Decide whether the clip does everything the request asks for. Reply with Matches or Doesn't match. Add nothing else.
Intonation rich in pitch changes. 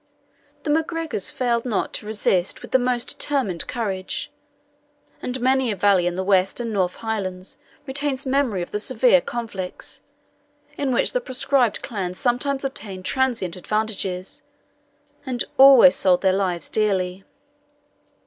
Matches